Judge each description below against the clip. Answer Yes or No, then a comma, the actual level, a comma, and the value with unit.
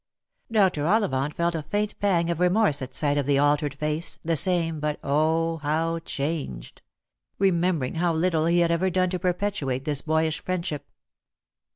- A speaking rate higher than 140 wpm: Yes, average, 175 wpm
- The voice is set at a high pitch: No, medium, 165 Hz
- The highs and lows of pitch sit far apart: No, average, 3.3 semitones